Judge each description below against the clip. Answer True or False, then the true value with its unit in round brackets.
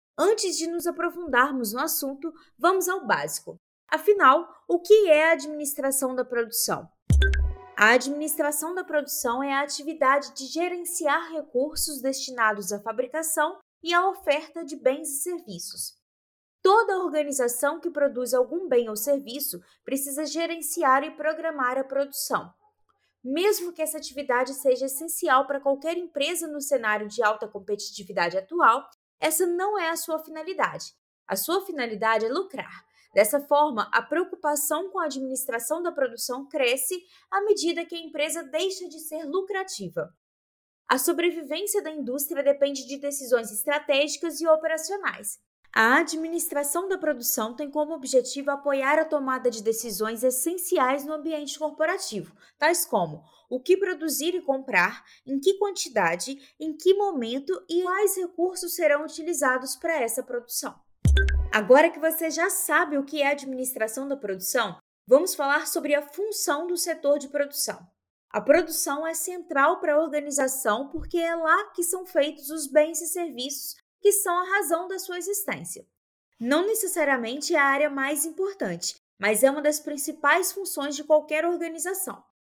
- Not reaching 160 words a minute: True (150 wpm)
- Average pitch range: True (4.1 semitones)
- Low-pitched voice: False (300 Hz)